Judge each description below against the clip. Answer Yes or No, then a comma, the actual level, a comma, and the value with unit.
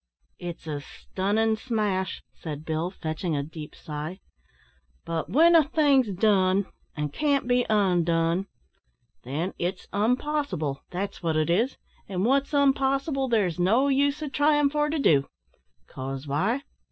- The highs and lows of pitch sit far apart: Yes, wide, 8.6 semitones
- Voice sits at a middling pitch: No, high, 195 Hz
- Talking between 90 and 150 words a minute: Yes, average, 140 wpm